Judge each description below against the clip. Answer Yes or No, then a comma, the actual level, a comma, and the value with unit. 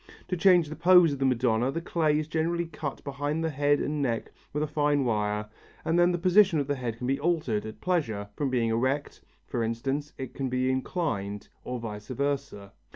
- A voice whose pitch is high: No, medium, 140 Hz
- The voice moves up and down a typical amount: Yes, average, 4.9 semitones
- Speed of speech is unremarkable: No, fast, 210 wpm